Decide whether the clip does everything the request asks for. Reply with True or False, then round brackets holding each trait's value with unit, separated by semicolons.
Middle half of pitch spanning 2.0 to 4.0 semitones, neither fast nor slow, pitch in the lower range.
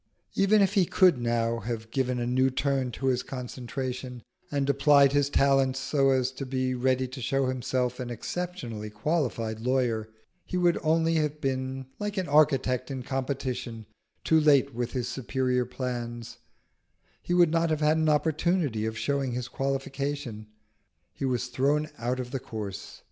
True (2.9 semitones; 165 wpm; 130 Hz)